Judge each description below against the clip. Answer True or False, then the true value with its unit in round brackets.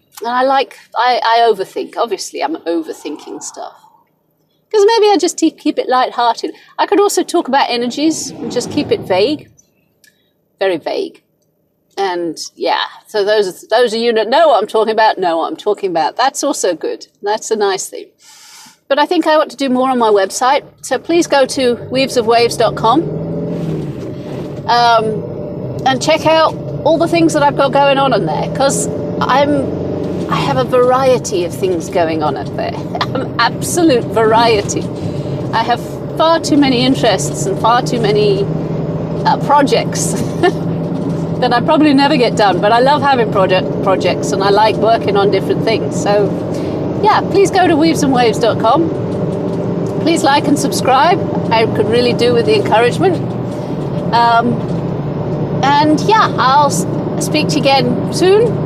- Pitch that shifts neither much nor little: False (8.4 semitones)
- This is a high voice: True (240 Hz)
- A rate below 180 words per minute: True (160 wpm)